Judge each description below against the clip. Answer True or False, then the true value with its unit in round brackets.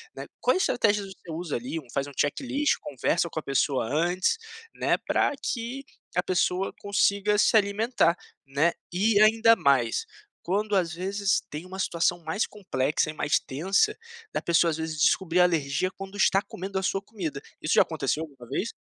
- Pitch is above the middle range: False (180 Hz)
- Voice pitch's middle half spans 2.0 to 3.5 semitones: False (4.6 semitones)